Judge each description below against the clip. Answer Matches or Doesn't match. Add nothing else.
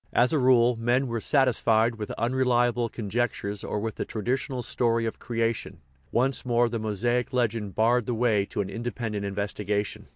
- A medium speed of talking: Matches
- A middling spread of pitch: Doesn't match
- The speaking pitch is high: Doesn't match